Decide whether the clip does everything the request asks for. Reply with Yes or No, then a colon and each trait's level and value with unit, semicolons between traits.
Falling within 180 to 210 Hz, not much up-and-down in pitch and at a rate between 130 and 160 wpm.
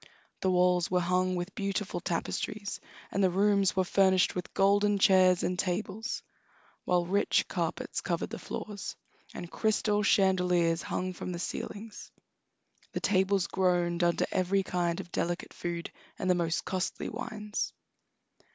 Yes: medium, 185 Hz; narrow, 2.0 semitones; average, 140 wpm